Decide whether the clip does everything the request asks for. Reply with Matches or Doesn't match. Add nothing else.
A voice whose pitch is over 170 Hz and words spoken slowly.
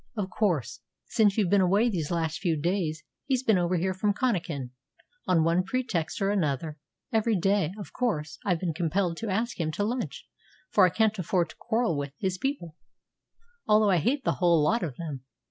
Doesn't match